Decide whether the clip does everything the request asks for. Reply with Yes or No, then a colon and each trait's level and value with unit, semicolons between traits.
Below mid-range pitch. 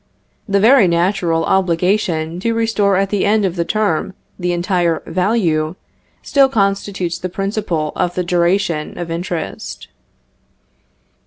No: medium, 185 Hz